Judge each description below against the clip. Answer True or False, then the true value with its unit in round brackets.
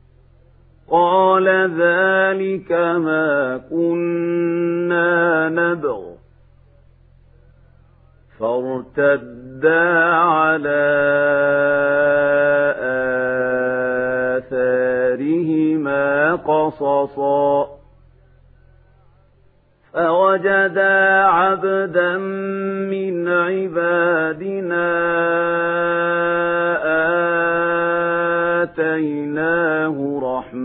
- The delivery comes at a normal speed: False (30 wpm)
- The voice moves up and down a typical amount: True (4.0 semitones)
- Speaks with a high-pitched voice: False (160 Hz)